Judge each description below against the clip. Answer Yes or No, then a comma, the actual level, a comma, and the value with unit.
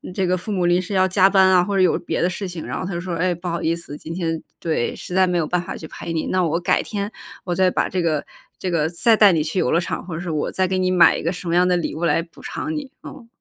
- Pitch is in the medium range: Yes, medium, 180 Hz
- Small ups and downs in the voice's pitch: Yes, narrow, 1.9 semitones